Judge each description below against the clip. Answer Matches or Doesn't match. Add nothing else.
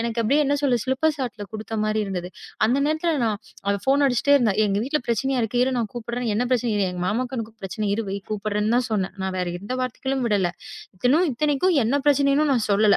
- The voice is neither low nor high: Doesn't match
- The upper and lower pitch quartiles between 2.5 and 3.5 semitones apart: Doesn't match